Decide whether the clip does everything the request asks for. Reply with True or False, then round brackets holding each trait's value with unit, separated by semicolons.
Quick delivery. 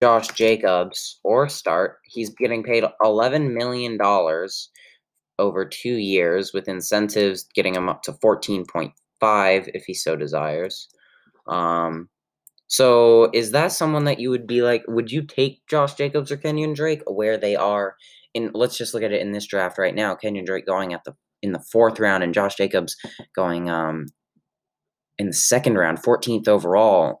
False (170 wpm)